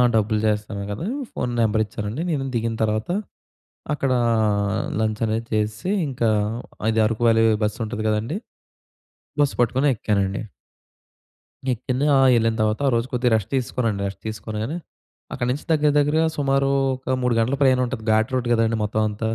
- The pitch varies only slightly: No, average, 3.1 semitones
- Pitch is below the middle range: Yes, low, 115 Hz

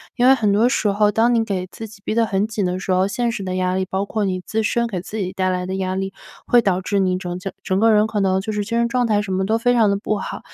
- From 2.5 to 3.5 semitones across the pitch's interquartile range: Yes, average, 2.9 semitones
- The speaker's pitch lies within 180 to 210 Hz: Yes, high, 200 Hz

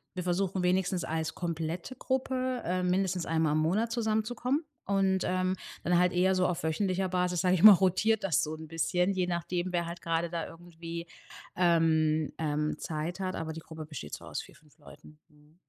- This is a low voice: No, medium, 175 Hz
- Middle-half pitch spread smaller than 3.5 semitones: Yes, average, 2.7 semitones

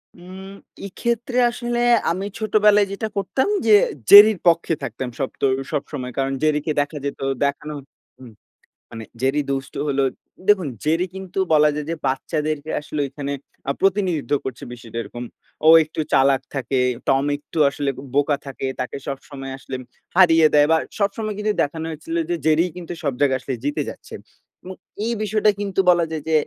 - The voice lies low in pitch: No, medium, 155 Hz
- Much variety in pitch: Yes, wide, 5.8 semitones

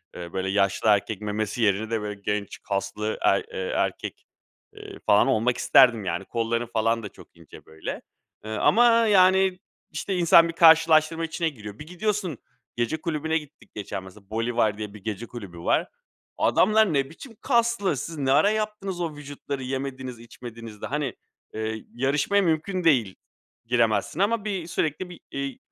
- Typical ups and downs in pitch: No, wide, 8.0 semitones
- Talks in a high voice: No, low, 135 Hz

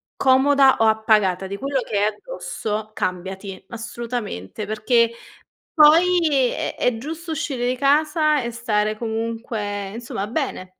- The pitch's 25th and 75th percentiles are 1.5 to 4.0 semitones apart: No, average, 4.7 semitones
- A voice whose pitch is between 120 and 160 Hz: No, high, 235 Hz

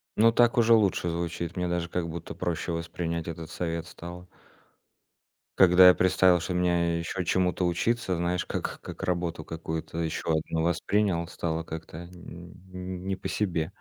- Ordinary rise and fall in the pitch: No, narrow, 1.7 semitones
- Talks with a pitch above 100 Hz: No, very low, 85 Hz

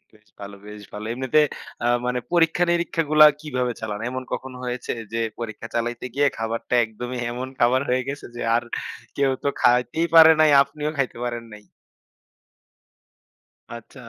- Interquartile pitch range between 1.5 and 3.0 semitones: No, average, 3.6 semitones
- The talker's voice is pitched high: No, low, 125 Hz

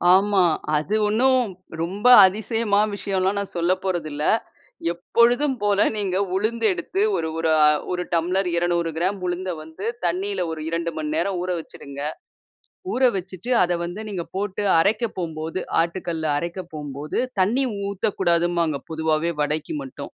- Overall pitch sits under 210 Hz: Yes, medium, 185 Hz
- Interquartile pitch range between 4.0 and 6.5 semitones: No, average, 3.5 semitones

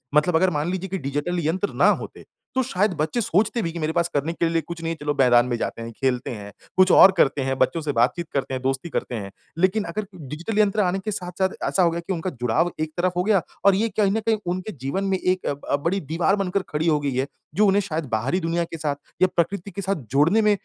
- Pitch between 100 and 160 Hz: No, medium, 170 Hz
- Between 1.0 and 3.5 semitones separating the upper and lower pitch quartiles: No, average, 4.8 semitones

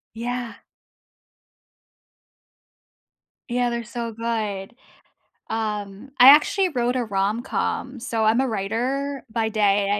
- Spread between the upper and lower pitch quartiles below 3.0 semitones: Yes, narrow, 2.6 semitones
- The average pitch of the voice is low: No, high, 230 Hz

